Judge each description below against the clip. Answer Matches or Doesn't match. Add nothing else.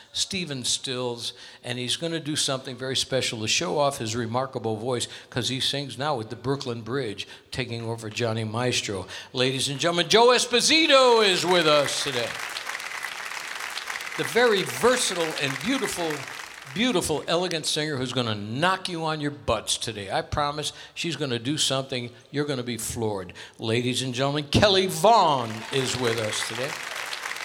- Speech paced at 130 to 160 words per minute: Matches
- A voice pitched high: Doesn't match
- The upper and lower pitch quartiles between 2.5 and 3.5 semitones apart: Doesn't match